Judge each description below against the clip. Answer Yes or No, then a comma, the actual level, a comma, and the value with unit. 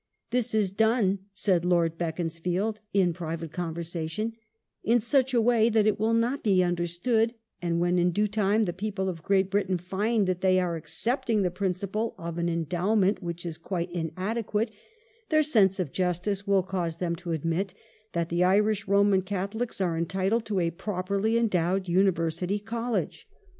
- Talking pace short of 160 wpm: No, average, 170 wpm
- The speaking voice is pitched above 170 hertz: Yes, high, 190 Hz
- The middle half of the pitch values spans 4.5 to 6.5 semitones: No, average, 3.7 semitones